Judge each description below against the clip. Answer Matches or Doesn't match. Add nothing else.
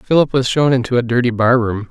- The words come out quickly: Matches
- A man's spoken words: Matches